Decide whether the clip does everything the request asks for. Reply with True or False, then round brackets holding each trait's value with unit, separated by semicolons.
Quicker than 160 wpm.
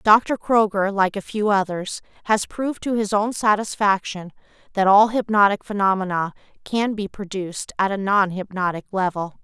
False (155 wpm)